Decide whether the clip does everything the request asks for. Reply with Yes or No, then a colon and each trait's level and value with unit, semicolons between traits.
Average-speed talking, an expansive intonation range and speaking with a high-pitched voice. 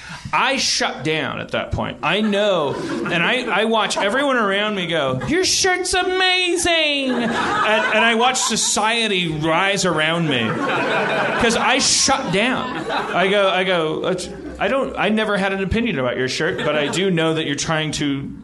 Yes: average, 170 wpm; wide, 7.0 semitones; high, 195 Hz